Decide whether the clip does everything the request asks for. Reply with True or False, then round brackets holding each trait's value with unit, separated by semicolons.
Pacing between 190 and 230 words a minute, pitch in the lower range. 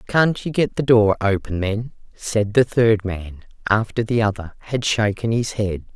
False (180 wpm; 110 Hz)